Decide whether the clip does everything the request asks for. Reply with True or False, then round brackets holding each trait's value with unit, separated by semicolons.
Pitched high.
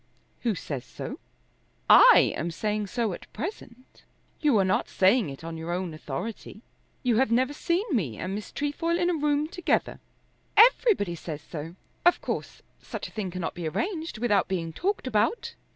True (215 Hz)